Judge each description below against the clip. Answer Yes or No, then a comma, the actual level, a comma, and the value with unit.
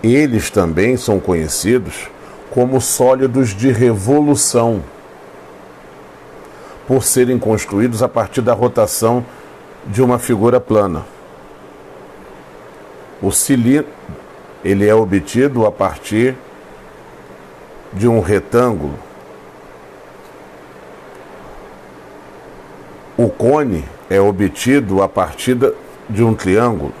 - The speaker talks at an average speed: No, slow, 85 wpm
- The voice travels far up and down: No, average, 3.7 semitones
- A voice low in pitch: Yes, low, 115 Hz